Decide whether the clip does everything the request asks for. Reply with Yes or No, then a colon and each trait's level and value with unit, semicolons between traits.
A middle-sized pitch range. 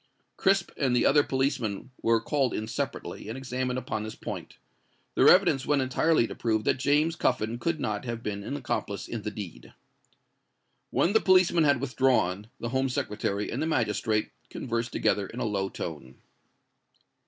Yes: average, 4.4 semitones